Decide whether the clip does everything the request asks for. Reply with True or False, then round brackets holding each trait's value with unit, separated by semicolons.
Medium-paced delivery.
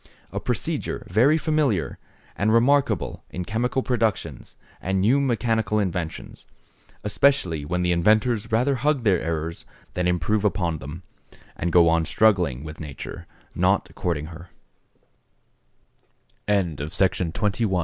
False (125 wpm)